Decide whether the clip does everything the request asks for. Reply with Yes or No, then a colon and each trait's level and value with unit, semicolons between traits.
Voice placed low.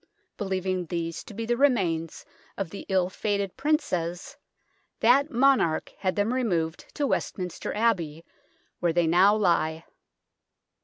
No: high, 190 Hz